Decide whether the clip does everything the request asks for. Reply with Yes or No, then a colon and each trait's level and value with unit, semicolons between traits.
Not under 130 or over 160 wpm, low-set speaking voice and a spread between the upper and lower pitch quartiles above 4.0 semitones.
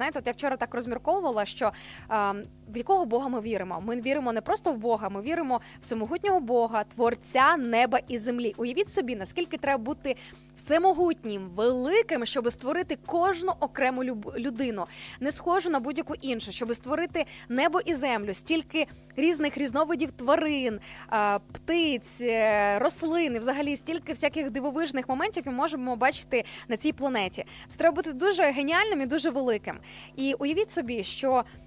No: average, 150 wpm; very high, 275 Hz; average, 5.2 semitones